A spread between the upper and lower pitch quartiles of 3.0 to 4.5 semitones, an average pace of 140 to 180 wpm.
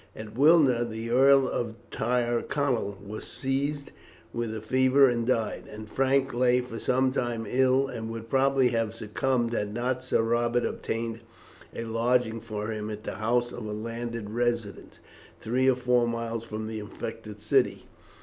No: narrow, 2.4 semitones; average, 160 wpm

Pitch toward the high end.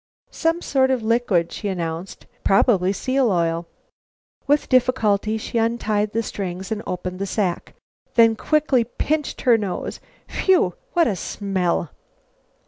Yes: high, 215 Hz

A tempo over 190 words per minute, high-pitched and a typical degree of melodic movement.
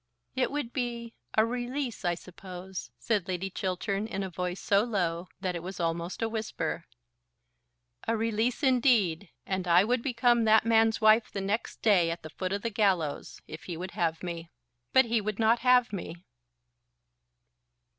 No: average, 170 wpm; high, 205 Hz; average, 4.4 semitones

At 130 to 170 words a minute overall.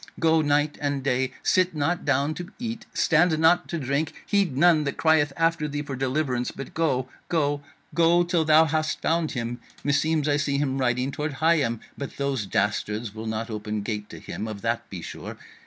No: average, 190 wpm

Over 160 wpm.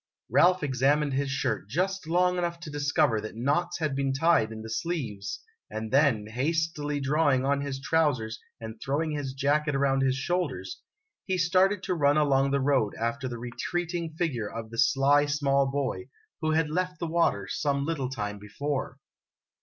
Yes: average, 175 wpm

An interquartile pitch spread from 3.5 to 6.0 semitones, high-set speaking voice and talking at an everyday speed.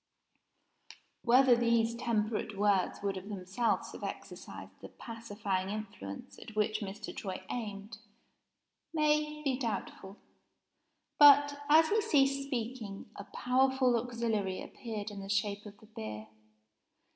No: average, 4.0 semitones; high, 220 Hz; slow, 120 wpm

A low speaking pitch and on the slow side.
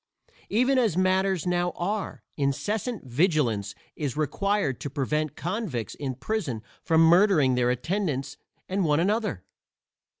No: medium, 165 Hz; slow, 125 wpm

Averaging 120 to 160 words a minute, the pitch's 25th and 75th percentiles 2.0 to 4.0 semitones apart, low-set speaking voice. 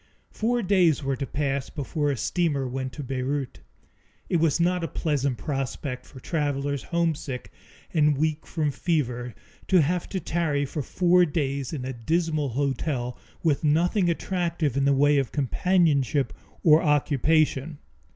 No: average, 150 wpm; average, 3.5 semitones; medium, 145 Hz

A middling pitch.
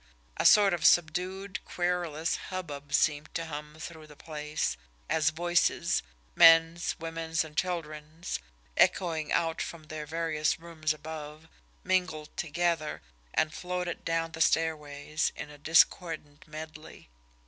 Yes: medium, 160 Hz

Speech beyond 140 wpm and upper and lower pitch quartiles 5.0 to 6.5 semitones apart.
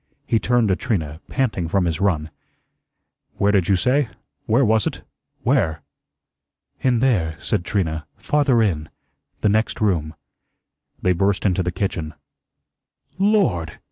No: slow, 135 wpm; wide, 5.6 semitones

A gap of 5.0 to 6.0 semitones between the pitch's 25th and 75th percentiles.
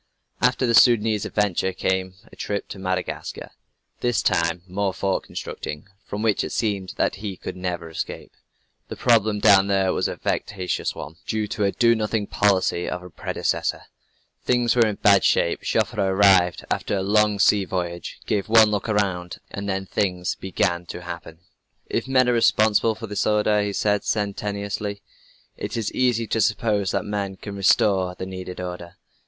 No: narrow, 2.5 semitones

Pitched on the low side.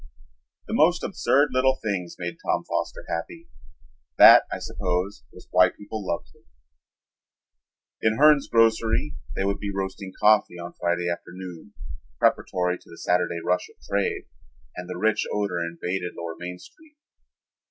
Yes: very low, 95 Hz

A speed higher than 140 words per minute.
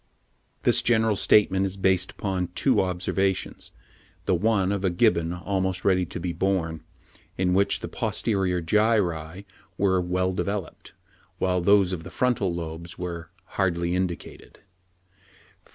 No: slow, 135 wpm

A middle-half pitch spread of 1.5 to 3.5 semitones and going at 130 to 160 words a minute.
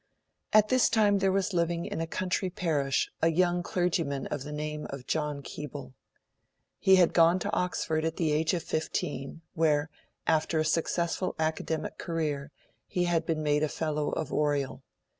No: average, 2.8 semitones; average, 170 wpm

